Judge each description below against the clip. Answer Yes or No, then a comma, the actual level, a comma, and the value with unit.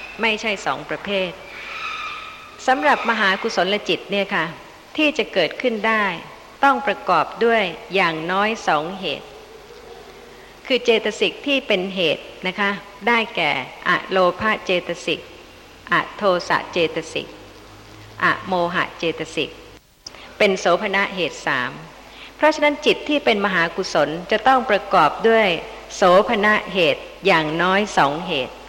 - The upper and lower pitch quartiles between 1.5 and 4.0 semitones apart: No, wide, 5.5 semitones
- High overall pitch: Yes, high, 205 Hz